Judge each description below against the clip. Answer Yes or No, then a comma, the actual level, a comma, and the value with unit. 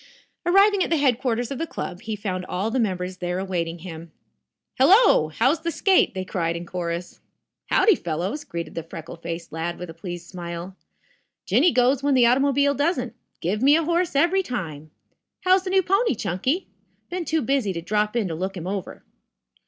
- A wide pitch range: Yes, wide, 8.7 semitones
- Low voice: No, high, 210 Hz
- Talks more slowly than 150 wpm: No, average, 185 wpm